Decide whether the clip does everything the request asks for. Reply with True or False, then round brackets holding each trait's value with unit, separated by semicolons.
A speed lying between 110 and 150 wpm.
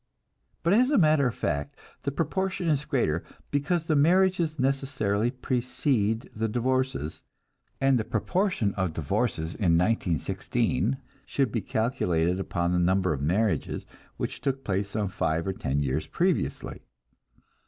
True (140 wpm)